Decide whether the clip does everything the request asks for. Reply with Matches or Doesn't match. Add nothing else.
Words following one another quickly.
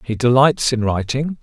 Doesn't match